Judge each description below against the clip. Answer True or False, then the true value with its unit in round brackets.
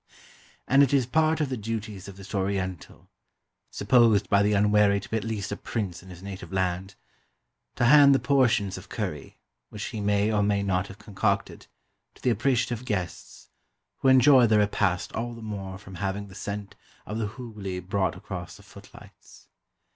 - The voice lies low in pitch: True (105 Hz)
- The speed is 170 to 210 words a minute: True (180 wpm)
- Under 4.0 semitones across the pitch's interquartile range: True (3.3 semitones)